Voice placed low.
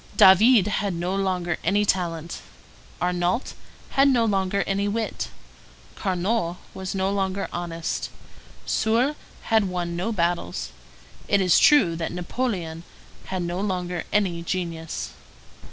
No: medium, 185 Hz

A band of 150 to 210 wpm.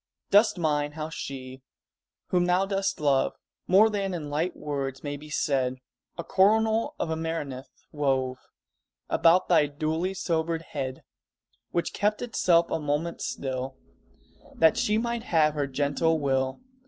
No: average, 140 wpm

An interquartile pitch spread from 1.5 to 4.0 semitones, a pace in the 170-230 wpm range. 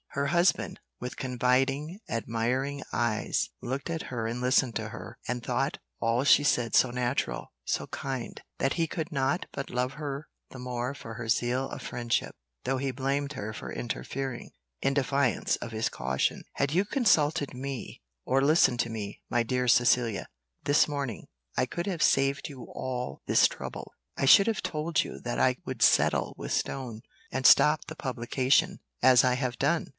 Yes: average, 2.7 semitones; average, 175 wpm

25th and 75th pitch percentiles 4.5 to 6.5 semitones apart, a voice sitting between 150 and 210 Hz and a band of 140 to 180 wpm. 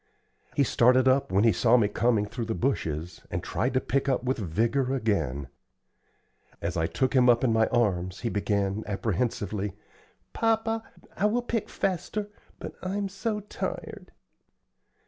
No: average, 5.2 semitones; low, 120 Hz; average, 150 wpm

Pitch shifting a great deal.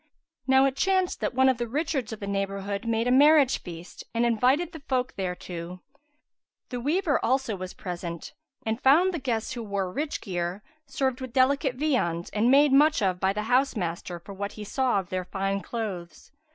Yes: wide, 5.7 semitones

